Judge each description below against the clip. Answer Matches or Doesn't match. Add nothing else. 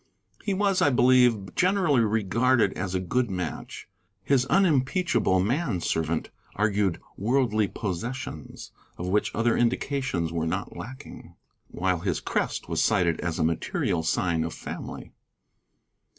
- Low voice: Matches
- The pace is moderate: Doesn't match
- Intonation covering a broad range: Matches